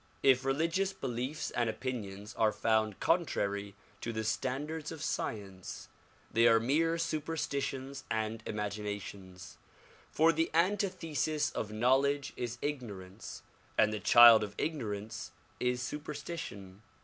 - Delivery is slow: Yes, slow, 120 wpm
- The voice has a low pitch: Yes, low, 125 Hz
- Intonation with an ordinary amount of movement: No, wide, 5.9 semitones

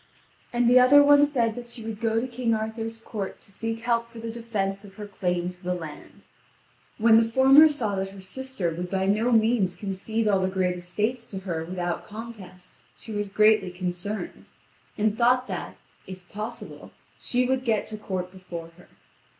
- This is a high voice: Yes, high, 215 Hz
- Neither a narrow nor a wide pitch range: Yes, average, 3.7 semitones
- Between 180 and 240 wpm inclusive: Yes, average, 185 wpm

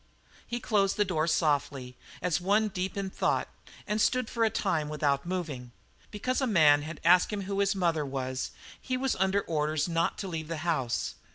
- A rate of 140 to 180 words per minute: No, average, 190 wpm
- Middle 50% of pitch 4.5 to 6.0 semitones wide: Yes, average, 4.9 semitones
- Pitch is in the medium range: Yes, medium, 175 Hz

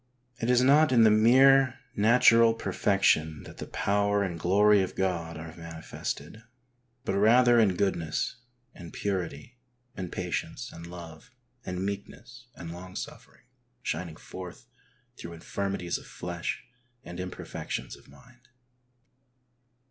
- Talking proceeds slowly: Yes, slow, 125 wpm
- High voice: No, very low, 95 Hz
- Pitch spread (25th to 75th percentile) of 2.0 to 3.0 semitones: No, average, 5.1 semitones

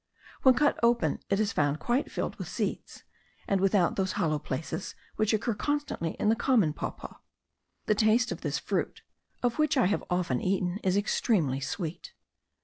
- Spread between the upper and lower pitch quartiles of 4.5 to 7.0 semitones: Yes, average, 5.2 semitones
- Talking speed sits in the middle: Yes, average, 170 wpm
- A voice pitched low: No, high, 200 Hz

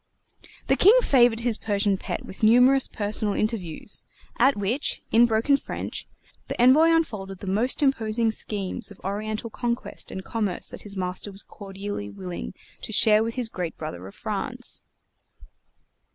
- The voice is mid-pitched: No, high, 215 Hz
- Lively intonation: No, average, 3.6 semitones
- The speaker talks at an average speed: Yes, average, 150 wpm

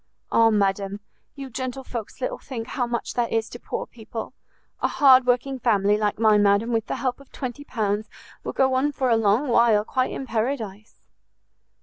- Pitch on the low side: No, high, 235 Hz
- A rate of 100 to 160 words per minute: No, average, 185 wpm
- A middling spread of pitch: Yes, average, 3.3 semitones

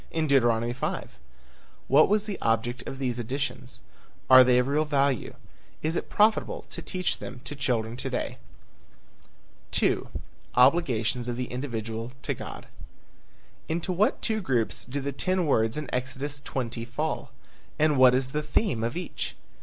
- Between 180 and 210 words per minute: No, average, 155 wpm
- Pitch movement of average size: Yes, average, 3.9 semitones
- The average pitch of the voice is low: Yes, low, 130 Hz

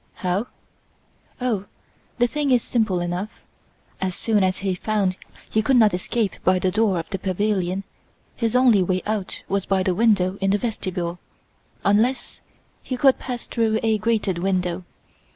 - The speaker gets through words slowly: No, average, 160 wpm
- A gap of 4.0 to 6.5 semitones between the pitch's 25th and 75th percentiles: No, average, 3.5 semitones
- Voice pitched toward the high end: Yes, high, 200 Hz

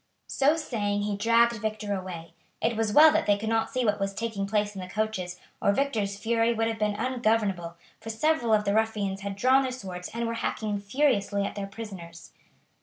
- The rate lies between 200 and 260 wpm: Yes, fast, 205 wpm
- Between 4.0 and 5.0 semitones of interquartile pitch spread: No, narrow, 2.5 semitones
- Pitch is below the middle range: No, high, 215 Hz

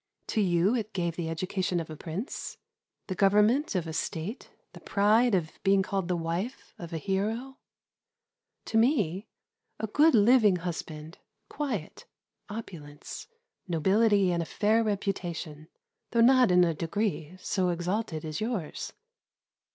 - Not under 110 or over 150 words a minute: Yes, average, 140 wpm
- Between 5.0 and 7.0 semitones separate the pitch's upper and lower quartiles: No, average, 4.6 semitones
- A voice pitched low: No, high, 190 Hz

